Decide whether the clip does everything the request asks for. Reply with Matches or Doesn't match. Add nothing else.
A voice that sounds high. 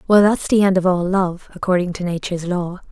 Doesn't match